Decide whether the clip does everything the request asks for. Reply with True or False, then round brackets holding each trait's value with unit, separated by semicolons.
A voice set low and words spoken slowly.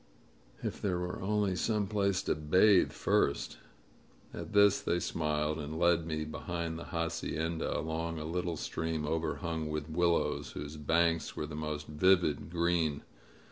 False (80 Hz; 150 wpm)